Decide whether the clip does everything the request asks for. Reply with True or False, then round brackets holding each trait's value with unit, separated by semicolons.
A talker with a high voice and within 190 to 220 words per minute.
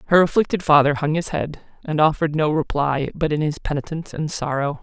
False (155 Hz; 200 wpm)